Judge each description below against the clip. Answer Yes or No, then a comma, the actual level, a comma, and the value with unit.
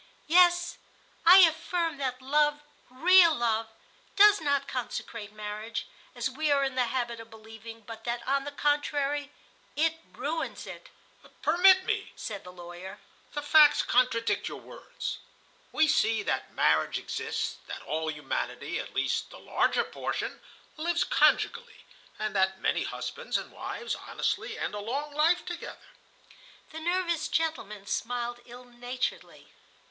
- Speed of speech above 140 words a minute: No, slow, 135 wpm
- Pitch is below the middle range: No, very high, 275 Hz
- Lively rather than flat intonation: Yes, wide, 6.0 semitones